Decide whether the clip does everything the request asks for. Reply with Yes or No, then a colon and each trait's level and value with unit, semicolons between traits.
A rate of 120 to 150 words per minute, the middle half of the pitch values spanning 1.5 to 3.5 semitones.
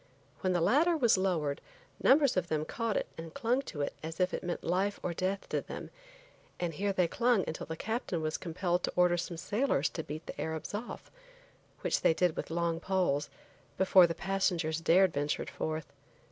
No: average, 195 wpm; average, 3.2 semitones